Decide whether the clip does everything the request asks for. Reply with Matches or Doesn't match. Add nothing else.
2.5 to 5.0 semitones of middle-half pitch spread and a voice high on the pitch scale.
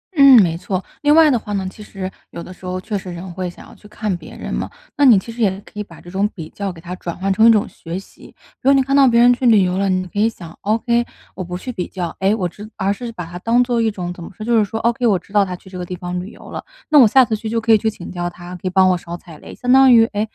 Matches